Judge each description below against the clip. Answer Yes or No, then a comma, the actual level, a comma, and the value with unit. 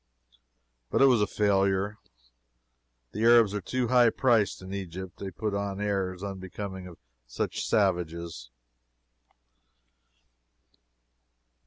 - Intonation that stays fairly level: Yes, narrow, 2.1 semitones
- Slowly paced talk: Yes, slow, 110 wpm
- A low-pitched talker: Yes, low, 100 Hz